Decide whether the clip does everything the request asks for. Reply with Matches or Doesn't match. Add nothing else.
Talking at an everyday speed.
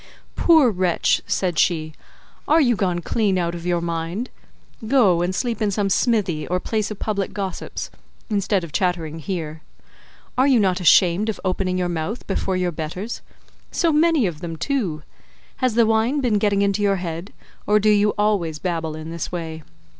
Matches